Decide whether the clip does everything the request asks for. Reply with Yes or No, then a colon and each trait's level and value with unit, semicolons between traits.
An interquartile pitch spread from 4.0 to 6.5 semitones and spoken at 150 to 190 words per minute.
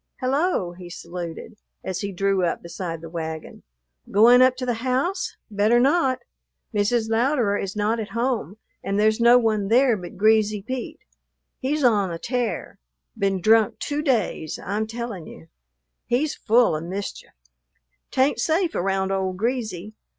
Yes: average, 4.4 semitones; average, 155 wpm